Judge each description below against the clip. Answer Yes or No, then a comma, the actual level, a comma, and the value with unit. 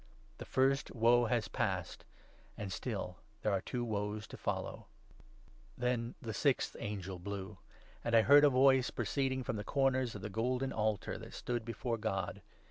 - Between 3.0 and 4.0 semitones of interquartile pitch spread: Yes, average, 3.6 semitones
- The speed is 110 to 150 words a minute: No, average, 175 wpm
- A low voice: Yes, low, 115 Hz